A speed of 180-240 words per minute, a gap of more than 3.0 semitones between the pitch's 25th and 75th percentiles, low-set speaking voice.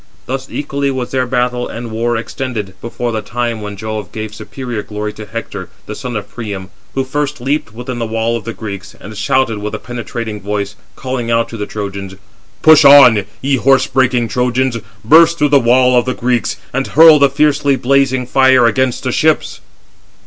Yes: average, 190 wpm; average, 3.4 semitones; low, 120 Hz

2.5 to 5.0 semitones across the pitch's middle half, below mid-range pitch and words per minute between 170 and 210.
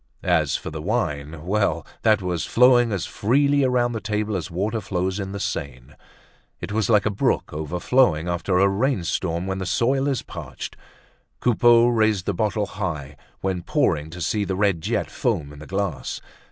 Yes: average, 4.5 semitones; low, 100 Hz; average, 180 wpm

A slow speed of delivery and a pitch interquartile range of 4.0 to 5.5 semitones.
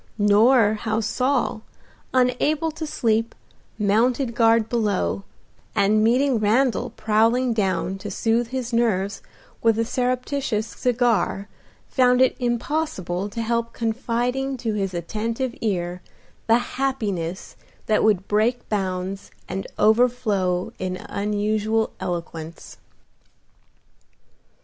No: slow, 105 wpm; average, 3.4 semitones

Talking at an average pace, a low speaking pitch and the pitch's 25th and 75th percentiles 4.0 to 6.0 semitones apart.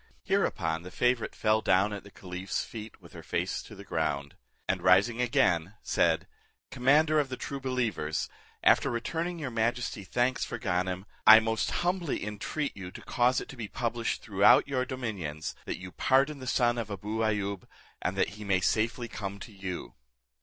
Yes: average, 180 wpm; low, 110 Hz; average, 4.7 semitones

